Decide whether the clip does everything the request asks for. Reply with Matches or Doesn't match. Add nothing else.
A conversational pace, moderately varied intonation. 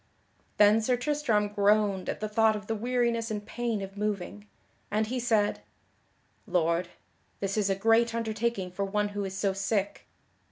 Doesn't match